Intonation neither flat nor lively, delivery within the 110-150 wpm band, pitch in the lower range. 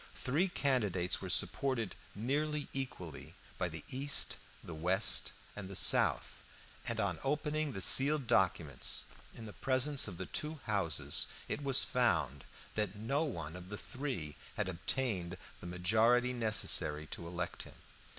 No: wide, 7.2 semitones; average, 145 wpm; low, 110 Hz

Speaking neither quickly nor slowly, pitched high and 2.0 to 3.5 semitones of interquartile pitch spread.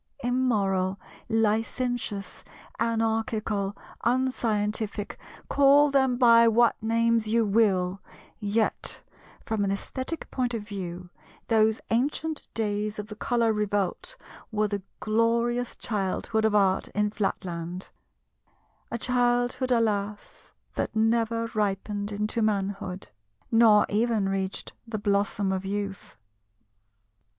No: slow, 100 wpm; high, 215 Hz; narrow, 2.5 semitones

